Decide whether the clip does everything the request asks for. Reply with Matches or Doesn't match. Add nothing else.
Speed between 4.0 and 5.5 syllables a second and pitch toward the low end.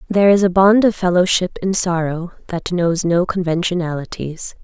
Doesn't match